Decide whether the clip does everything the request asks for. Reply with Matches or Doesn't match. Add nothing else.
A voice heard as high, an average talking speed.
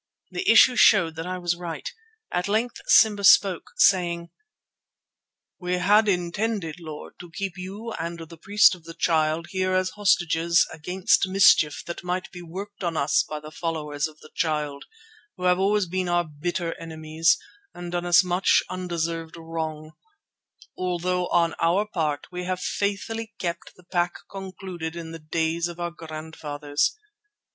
Doesn't match